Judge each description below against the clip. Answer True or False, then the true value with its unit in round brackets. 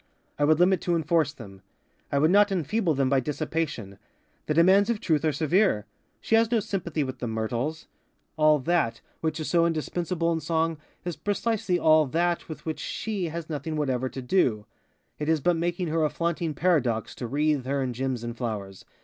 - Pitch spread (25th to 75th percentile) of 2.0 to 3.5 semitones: False (4.5 semitones)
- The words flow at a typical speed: True (190 wpm)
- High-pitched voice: False (155 Hz)